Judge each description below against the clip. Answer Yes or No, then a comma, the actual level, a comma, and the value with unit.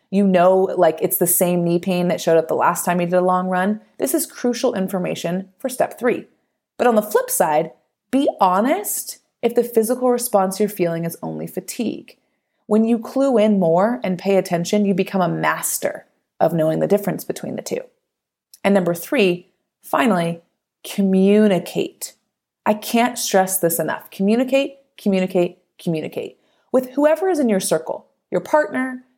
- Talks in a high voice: Yes, high, 195 Hz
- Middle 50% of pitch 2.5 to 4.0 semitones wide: No, wide, 5.5 semitones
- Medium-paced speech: Yes, average, 170 wpm